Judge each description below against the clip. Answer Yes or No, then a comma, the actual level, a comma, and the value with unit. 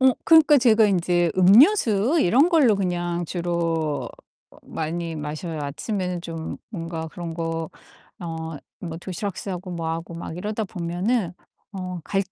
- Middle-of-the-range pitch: Yes, medium, 175 Hz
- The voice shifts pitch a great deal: No, average, 3.6 semitones